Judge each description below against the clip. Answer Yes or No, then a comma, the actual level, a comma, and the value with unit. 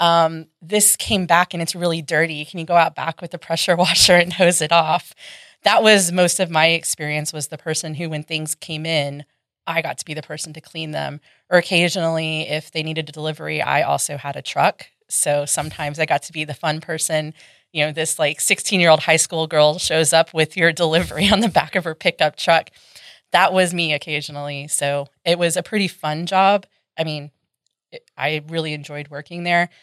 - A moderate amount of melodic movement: No, narrow, 2.2 semitones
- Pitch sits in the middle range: Yes, medium, 160 Hz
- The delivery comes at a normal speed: No, fast, 215 wpm